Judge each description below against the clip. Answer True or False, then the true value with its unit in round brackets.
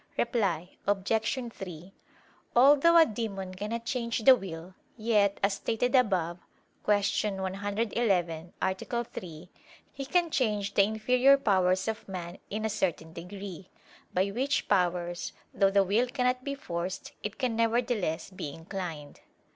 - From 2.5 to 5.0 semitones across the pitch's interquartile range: True (4.3 semitones)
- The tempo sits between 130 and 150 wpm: True (135 wpm)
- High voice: True (200 Hz)